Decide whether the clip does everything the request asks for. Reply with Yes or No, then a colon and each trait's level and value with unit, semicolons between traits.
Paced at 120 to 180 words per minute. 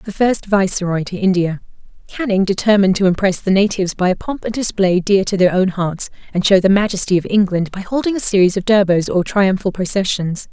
No: fast, 205 wpm